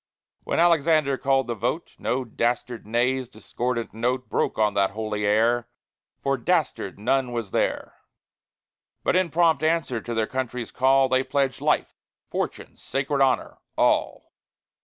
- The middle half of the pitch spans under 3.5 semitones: Yes, average, 2.9 semitones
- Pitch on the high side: No, low, 130 Hz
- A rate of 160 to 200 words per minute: No, average, 140 wpm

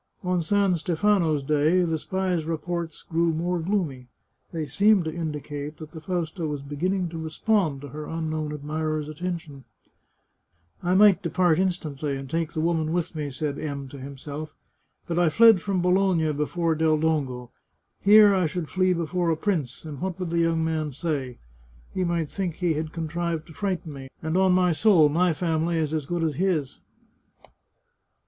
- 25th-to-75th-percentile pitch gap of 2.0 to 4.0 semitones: Yes, average, 2.9 semitones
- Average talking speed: Yes, average, 180 wpm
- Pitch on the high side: No, medium, 160 Hz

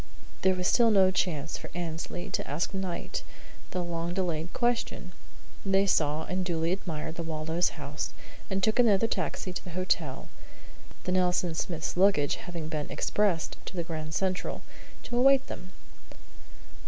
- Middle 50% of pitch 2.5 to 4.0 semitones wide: Yes, average, 2.9 semitones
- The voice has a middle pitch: Yes, medium, 180 Hz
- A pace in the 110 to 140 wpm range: No, average, 155 wpm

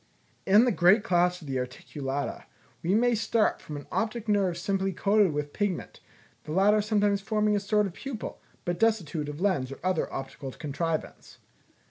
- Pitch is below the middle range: No, high, 190 Hz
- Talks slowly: No, average, 170 wpm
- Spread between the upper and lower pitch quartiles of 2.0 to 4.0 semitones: No, average, 5.3 semitones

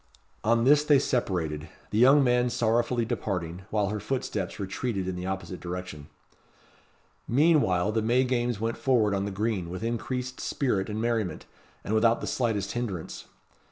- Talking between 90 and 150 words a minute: No, average, 160 wpm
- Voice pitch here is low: Yes, low, 110 Hz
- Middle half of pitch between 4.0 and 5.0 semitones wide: Yes, average, 4.4 semitones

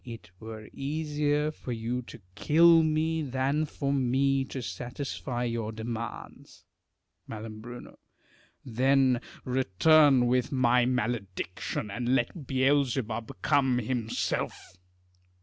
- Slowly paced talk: Yes, slow, 100 wpm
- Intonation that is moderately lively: Yes, average, 3.2 semitones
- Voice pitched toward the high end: No, low, 125 Hz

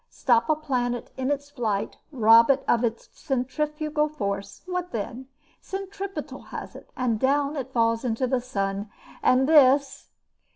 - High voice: Yes, very high, 260 Hz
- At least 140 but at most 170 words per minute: Yes, average, 150 wpm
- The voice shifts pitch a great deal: No, average, 4.2 semitones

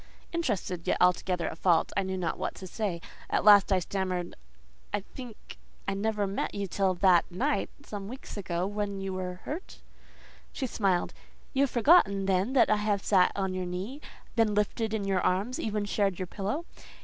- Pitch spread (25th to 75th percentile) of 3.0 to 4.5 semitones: No, narrow, 2.5 semitones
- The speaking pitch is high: Yes, high, 195 Hz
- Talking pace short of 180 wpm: No, average, 185 wpm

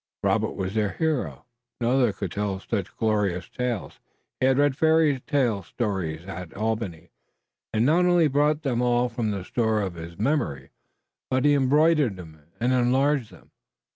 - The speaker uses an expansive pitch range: Yes, wide, 6.2 semitones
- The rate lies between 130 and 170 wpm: Yes, average, 160 wpm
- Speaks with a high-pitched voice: No, low, 120 Hz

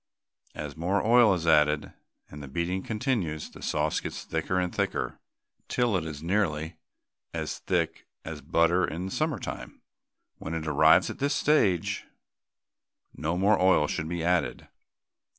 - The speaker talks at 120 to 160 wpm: Yes, average, 150 wpm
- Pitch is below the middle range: Yes, very low, 85 Hz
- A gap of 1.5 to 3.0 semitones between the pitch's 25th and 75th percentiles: No, average, 4.0 semitones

